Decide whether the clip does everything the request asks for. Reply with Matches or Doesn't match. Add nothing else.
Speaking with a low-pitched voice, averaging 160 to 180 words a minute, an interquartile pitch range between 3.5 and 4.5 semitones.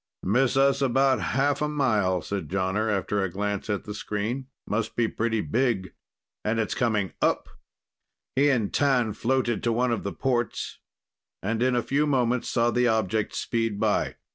Matches